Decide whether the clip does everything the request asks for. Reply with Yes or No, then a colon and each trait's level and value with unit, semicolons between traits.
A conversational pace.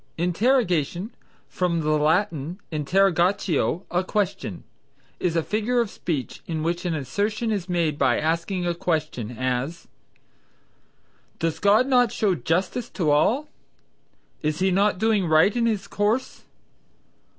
No: slow, 130 wpm